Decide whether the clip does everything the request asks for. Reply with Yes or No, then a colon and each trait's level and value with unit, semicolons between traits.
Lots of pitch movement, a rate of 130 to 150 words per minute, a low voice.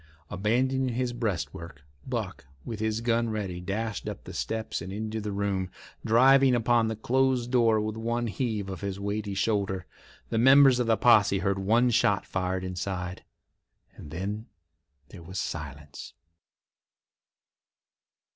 No: average, 3.7 semitones; average, 140 wpm; low, 110 Hz